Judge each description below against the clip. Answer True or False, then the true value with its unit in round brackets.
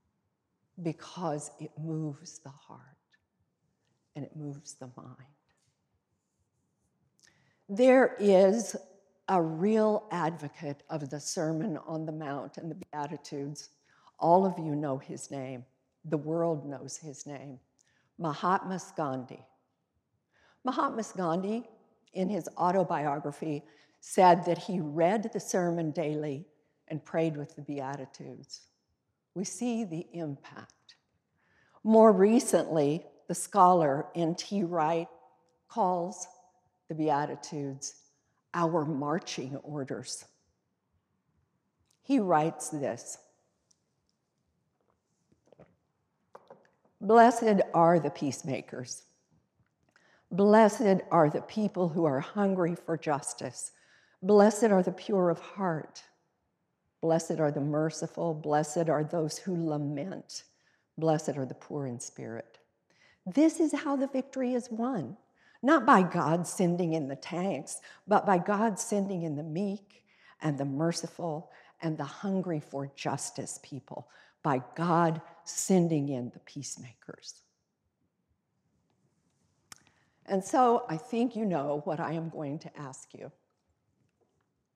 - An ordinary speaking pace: False (110 wpm)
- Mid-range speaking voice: True (165 Hz)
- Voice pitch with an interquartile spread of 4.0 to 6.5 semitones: True (4.4 semitones)